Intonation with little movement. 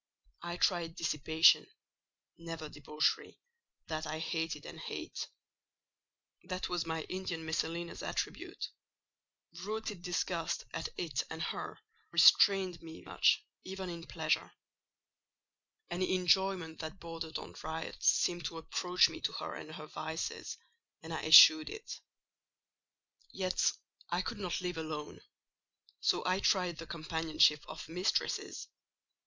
Yes: narrow, 2.3 semitones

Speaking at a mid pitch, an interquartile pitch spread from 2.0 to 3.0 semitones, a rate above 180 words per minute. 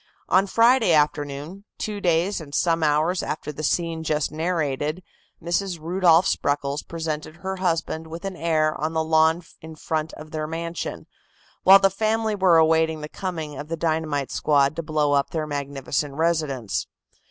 No: medium, 160 Hz; narrow, 2.4 semitones; average, 165 wpm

